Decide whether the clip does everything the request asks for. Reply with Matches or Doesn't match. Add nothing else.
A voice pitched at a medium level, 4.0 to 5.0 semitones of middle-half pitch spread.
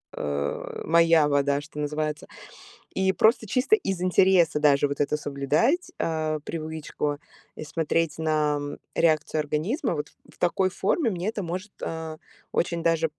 Doesn't match